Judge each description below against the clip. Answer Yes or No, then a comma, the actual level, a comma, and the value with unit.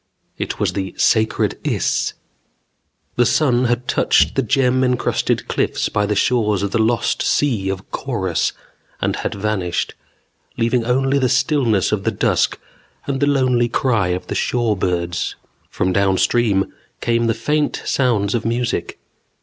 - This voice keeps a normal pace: Yes, average, 145 wpm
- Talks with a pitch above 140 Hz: No, low, 115 Hz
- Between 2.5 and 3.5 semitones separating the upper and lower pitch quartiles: No, average, 4.1 semitones